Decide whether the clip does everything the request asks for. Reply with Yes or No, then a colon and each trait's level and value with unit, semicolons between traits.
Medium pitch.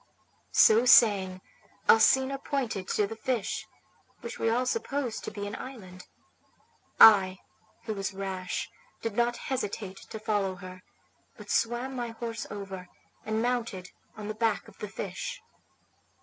No: high, 220 Hz